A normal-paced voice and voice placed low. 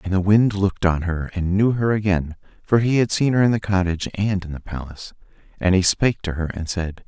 No: fast, 245 wpm; very low, 95 Hz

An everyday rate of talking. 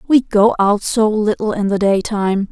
Yes: average, 190 wpm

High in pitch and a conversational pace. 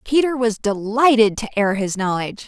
Yes: high, 225 Hz; average, 170 wpm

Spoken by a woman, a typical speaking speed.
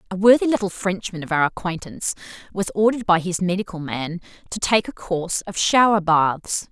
Yes: female; average, 180 wpm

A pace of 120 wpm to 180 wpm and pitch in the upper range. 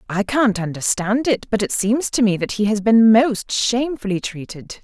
No: average, 200 wpm; high, 220 Hz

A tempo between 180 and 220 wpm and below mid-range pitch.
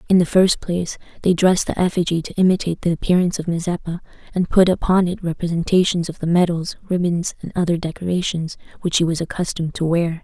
No: average, 190 wpm; medium, 175 Hz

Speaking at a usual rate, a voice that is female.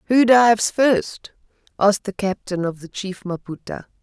Yes: average, 150 wpm; female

